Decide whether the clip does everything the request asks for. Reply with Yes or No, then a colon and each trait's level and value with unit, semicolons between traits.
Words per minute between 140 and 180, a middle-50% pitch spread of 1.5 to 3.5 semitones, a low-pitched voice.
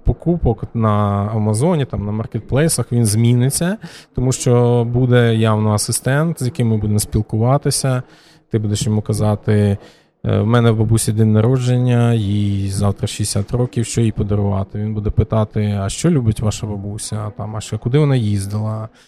Yes: fast, 155 wpm; average, 2.7 semitones; low, 110 Hz